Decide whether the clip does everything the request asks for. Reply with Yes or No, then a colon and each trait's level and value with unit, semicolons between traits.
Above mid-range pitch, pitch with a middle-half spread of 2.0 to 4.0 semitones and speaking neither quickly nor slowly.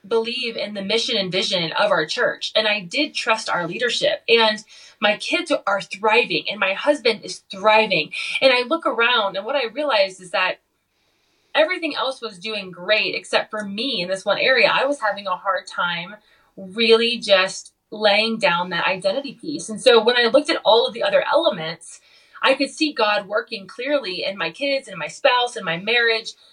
No: high, 225 Hz; wide, 5.6 semitones; average, 195 wpm